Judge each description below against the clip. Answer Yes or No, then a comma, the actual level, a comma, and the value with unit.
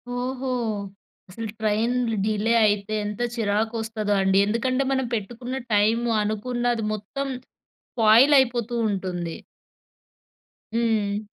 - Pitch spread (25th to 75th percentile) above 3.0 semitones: No, average, 2.7 semitones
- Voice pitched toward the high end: Yes, high, 225 Hz